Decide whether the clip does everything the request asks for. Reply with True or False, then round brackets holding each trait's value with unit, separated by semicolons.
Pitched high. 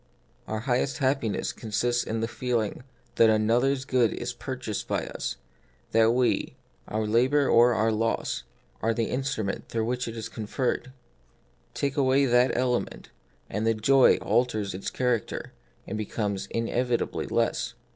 False (120 Hz)